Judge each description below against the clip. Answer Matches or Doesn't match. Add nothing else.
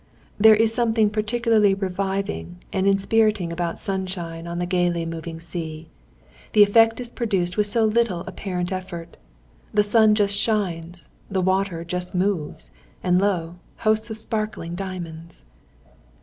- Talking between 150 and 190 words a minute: Doesn't match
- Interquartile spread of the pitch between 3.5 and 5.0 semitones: Matches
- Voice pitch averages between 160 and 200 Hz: Matches